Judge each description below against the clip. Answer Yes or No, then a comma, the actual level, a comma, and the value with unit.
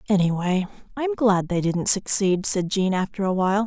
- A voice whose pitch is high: Yes, high, 195 Hz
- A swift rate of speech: No, average, 180 wpm